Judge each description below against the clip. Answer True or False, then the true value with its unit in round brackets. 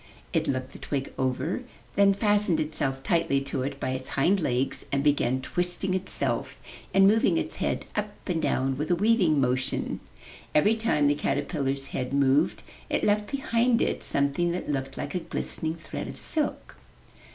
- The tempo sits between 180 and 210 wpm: False (170 wpm)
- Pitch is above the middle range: False (150 Hz)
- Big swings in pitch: True (6.2 semitones)